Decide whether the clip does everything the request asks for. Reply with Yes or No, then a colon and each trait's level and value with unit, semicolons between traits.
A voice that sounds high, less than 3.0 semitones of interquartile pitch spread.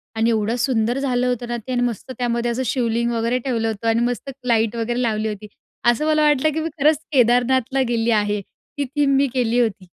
Yes: high, 240 Hz; narrow, 2.4 semitones